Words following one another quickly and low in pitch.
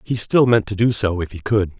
Yes: fast, 300 wpm; low, 105 Hz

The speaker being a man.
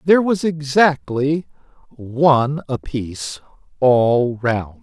Yes: male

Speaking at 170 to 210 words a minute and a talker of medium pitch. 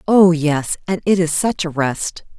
Yes: average, 200 wpm; medium, 170 Hz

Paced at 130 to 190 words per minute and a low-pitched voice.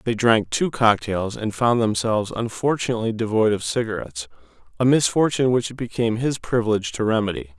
Yes: average, 160 wpm; low, 115 Hz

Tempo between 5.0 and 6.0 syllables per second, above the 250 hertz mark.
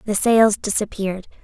No: 5.1 syllables/s; high, 205 Hz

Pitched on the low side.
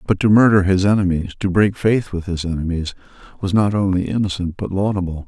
Yes: very low, 95 Hz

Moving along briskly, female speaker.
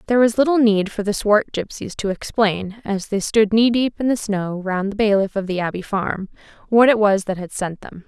Yes: fast, 240 wpm; female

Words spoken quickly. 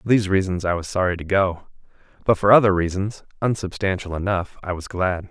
No: average, 190 wpm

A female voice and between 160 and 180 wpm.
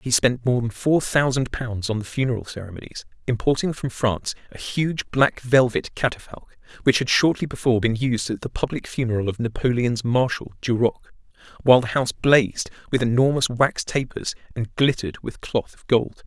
No: male; average, 175 wpm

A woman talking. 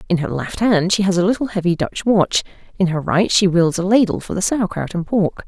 Yes: female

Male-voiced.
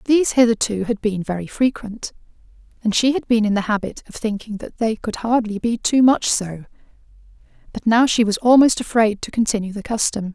No: female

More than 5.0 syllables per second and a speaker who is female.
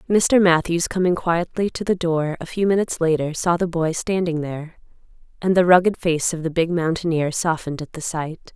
Yes: 5.3 syllables/s; female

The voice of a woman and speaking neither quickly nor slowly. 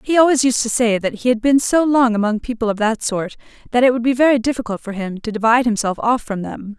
No: female; fast, 265 wpm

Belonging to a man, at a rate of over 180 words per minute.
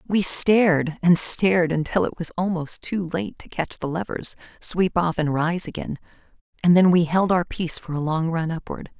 No: female; average, 200 wpm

